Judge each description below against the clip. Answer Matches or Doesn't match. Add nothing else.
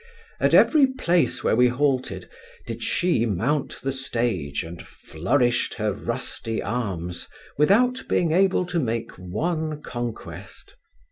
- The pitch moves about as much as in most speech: Doesn't match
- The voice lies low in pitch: Matches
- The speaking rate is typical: Doesn't match